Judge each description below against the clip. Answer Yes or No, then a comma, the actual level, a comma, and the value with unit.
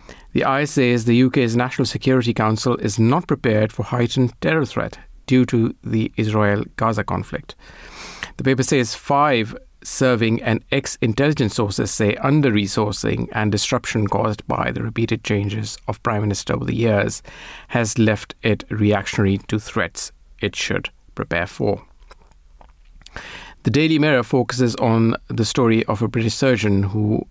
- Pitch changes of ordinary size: Yes, average, 3.1 semitones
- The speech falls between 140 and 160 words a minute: Yes, average, 150 wpm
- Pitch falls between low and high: No, low, 115 Hz